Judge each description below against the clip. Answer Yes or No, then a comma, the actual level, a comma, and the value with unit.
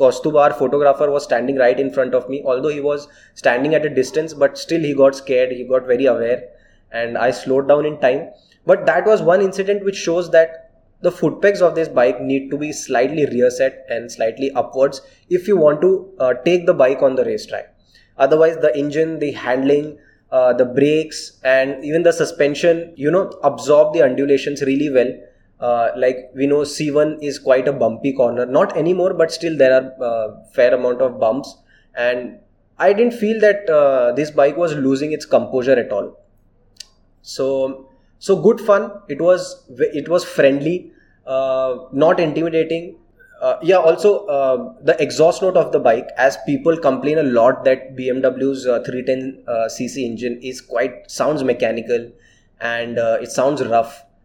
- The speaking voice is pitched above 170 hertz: No, medium, 140 Hz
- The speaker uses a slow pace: No, average, 180 wpm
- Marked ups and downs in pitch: No, average, 4.2 semitones